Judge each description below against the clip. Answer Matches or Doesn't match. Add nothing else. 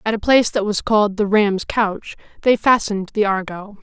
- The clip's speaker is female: Matches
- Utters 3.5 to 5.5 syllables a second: Matches